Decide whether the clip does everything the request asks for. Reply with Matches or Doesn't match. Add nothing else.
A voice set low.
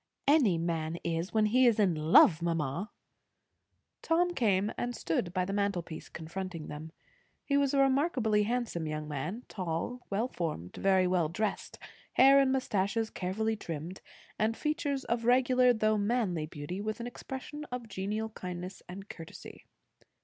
Doesn't match